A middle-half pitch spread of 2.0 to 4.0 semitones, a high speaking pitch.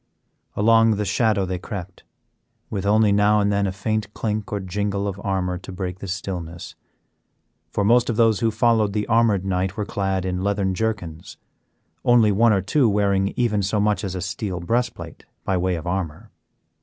No: narrow, 2.5 semitones; low, 100 Hz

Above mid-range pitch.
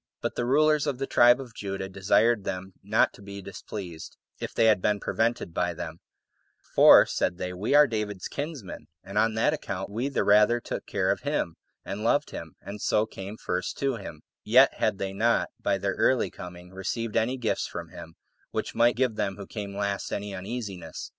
No: low, 105 Hz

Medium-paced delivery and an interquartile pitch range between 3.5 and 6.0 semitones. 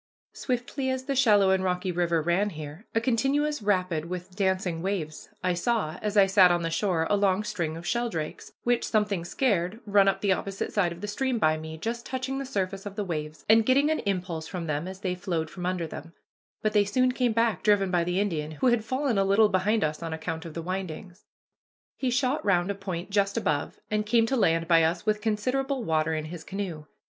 No: fast, 220 wpm; average, 4.5 semitones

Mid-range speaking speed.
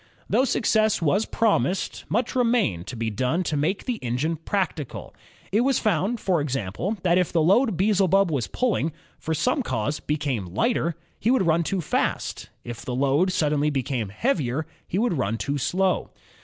Yes: average, 170 wpm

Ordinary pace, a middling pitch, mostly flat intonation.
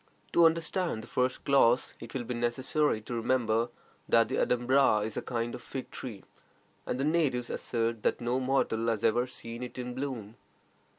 No: average, 180 wpm; low, 125 Hz; narrow, 2.2 semitones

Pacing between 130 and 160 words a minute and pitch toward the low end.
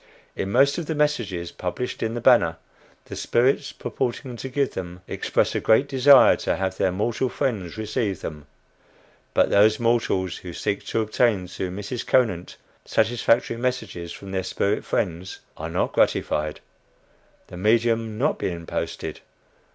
Yes: average, 150 wpm; low, 110 Hz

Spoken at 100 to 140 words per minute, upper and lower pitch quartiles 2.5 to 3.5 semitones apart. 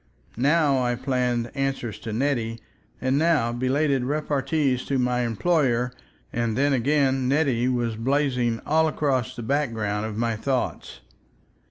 Yes: slow, 135 wpm; average, 3.1 semitones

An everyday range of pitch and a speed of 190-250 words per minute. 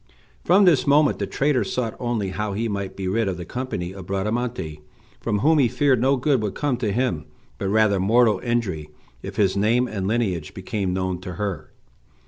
Yes: average, 4.5 semitones; average, 195 wpm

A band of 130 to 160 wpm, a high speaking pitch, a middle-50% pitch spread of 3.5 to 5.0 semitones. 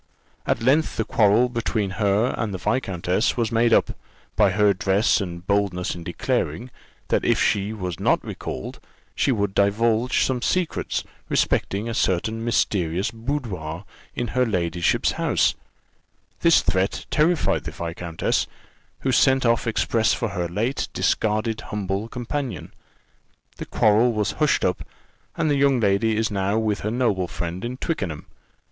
No: average, 150 wpm; low, 110 Hz; average, 3.9 semitones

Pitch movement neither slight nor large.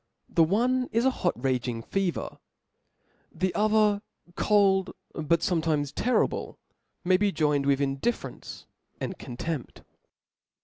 No: wide, 6.5 semitones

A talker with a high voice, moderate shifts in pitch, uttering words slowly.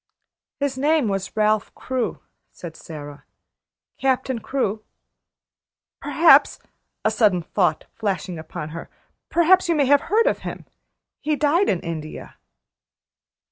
No: high, 225 Hz; wide, 8.4 semitones; slow, 120 wpm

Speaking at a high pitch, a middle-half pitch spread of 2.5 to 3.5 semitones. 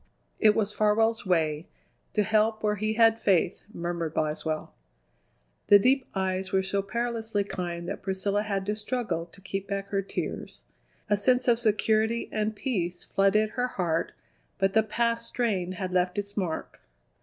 Yes: high, 205 Hz; average, 2.9 semitones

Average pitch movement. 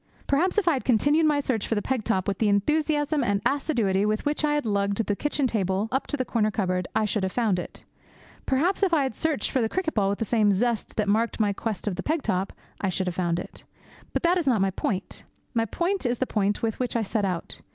No: wide, 6.2 semitones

